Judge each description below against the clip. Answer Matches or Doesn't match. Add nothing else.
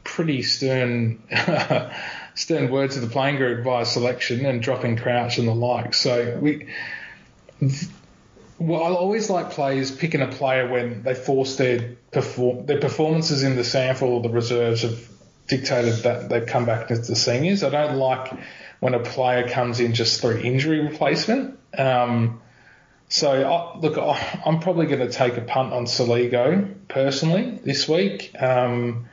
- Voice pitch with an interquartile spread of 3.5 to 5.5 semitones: Doesn't match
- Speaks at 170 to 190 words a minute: Doesn't match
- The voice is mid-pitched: Doesn't match